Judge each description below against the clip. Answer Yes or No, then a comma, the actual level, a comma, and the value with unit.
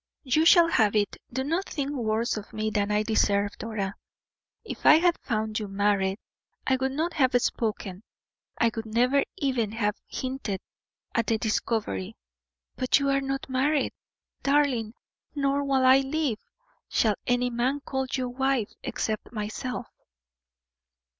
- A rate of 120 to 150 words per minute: Yes, average, 145 wpm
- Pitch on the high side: Yes, high, 245 Hz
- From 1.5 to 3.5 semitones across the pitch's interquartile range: No, average, 4.1 semitones